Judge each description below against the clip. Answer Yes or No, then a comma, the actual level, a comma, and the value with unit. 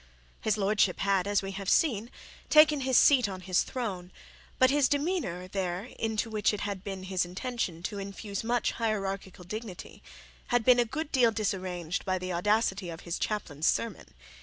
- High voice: Yes, high, 200 Hz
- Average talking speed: Yes, average, 175 wpm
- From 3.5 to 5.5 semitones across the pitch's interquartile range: Yes, average, 3.9 semitones